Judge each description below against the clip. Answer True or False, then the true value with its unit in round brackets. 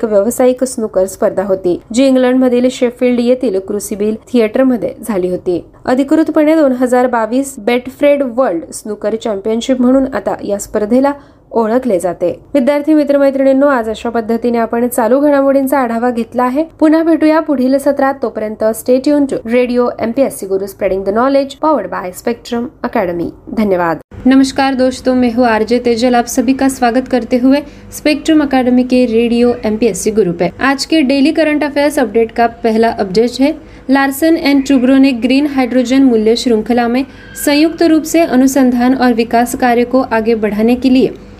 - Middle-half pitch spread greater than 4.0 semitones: False (3.1 semitones)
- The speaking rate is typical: False (160 wpm)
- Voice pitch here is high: True (250 Hz)